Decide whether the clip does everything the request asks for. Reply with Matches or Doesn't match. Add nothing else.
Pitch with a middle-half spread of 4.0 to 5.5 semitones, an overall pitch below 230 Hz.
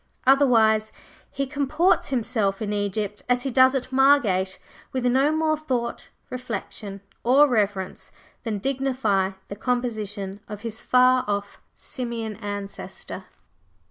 Doesn't match